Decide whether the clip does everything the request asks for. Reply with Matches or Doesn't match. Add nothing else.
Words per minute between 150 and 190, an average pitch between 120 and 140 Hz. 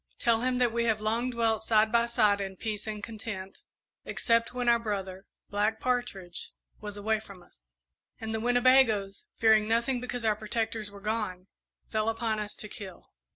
Doesn't match